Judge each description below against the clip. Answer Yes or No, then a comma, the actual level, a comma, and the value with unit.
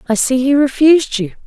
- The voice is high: Yes, very high, 265 Hz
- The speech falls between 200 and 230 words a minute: Yes, fast, 205 wpm